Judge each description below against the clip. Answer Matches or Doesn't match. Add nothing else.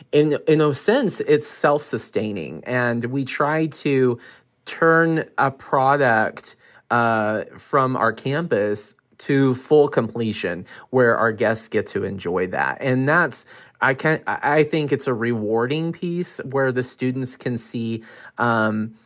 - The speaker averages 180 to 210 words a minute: Doesn't match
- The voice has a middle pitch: Doesn't match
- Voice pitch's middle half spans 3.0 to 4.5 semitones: Matches